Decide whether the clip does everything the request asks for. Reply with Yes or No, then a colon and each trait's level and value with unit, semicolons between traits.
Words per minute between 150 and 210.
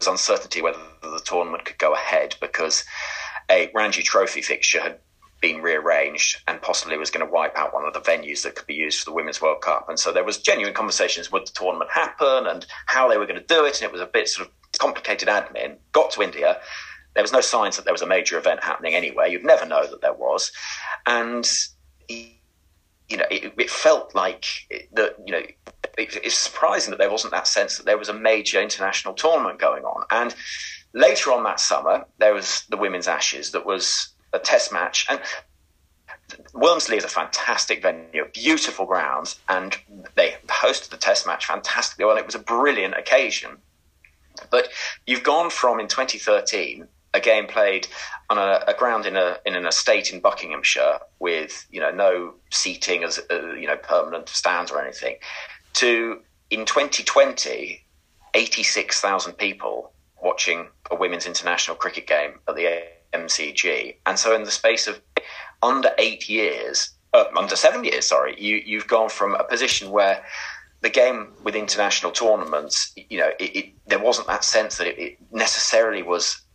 Yes: average, 180 wpm